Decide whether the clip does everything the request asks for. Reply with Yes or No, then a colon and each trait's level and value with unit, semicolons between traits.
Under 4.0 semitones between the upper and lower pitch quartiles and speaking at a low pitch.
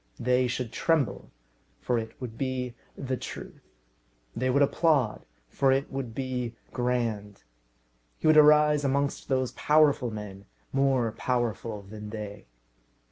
Yes: average, 3.5 semitones; low, 125 Hz